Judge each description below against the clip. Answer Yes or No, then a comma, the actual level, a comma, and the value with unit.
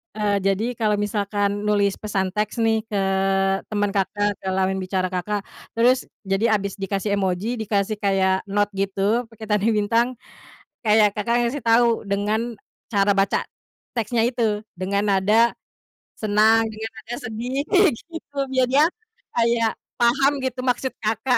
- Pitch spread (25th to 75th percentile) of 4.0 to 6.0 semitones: No, average, 2.7 semitones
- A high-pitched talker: Yes, high, 210 Hz